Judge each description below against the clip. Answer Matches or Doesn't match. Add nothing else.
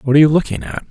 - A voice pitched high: Doesn't match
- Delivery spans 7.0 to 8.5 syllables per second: Matches